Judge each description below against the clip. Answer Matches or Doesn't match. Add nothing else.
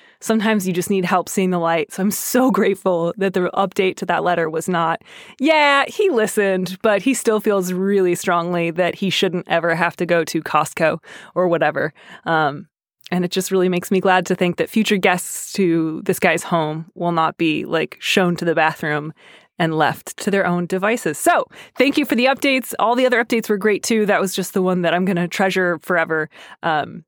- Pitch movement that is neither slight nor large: Matches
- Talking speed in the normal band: Doesn't match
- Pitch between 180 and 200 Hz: Matches